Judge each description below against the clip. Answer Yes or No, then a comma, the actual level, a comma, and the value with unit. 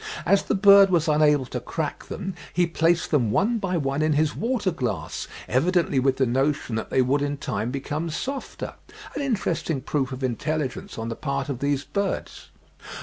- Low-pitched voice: No, medium, 150 Hz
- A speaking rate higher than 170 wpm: Yes, average, 180 wpm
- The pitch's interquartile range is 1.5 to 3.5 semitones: No, average, 5.1 semitones